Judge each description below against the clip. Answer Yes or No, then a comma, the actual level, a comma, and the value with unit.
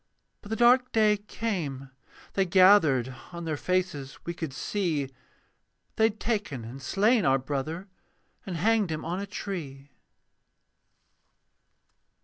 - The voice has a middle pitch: Yes, medium, 175 Hz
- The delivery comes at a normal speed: No, slow, 130 wpm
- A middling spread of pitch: No, wide, 6.7 semitones